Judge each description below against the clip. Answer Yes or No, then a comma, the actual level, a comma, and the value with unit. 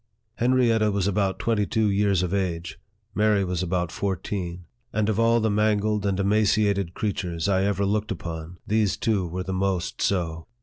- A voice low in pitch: Yes, low, 100 Hz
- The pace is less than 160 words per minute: No, average, 170 wpm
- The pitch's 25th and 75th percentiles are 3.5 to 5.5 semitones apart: No, average, 2.7 semitones